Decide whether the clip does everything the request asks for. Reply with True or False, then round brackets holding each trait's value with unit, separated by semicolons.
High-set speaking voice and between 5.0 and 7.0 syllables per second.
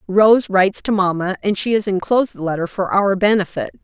True (195 Hz; 5.7 syllables/s)